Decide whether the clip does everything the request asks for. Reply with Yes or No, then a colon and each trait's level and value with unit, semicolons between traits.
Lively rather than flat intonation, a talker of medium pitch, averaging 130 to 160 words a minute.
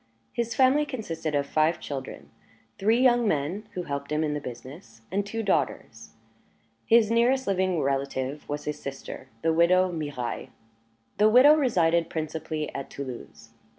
Yes: wide, 7.2 semitones; medium, 165 Hz; average, 150 wpm